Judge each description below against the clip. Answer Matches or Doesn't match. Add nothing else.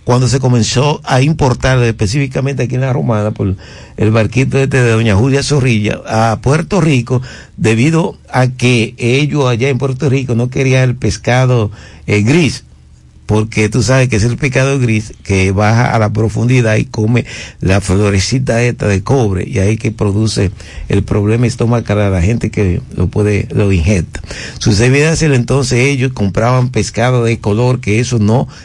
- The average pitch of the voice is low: Matches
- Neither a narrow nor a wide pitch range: Matches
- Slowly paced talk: Doesn't match